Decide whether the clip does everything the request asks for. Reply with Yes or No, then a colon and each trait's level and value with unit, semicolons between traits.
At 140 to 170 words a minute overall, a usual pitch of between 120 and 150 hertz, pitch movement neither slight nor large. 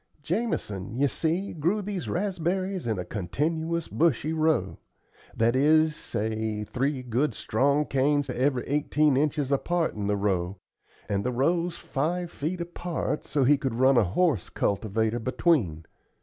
No: average, 145 wpm; medium, 140 Hz; wide, 6.7 semitones